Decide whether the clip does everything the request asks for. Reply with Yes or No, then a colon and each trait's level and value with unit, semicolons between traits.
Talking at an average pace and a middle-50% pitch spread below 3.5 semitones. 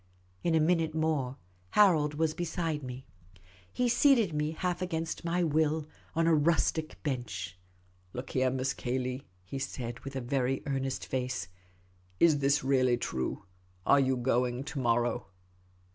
No: average, 160 wpm; average, 4.2 semitones